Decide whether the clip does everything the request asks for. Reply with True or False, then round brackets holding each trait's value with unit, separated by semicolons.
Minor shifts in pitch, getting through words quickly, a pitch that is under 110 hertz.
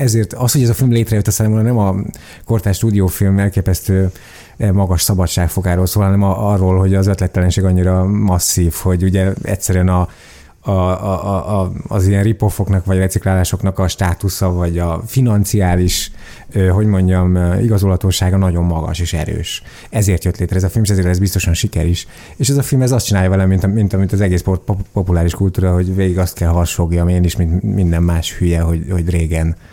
True (2.1 semitones; 190 wpm; 95 Hz)